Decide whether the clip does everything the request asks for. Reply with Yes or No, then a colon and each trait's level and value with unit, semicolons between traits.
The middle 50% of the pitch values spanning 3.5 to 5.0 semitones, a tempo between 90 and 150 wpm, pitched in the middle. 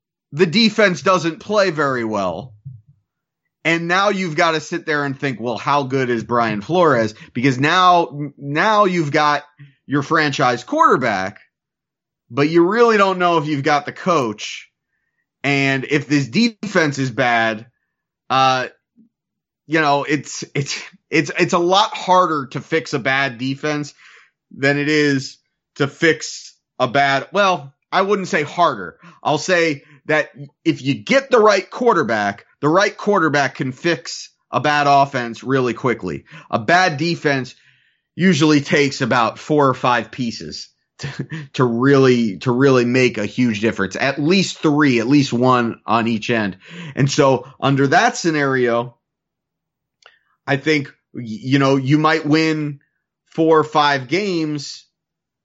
Yes: average, 3.8 semitones; average, 145 wpm; medium, 145 Hz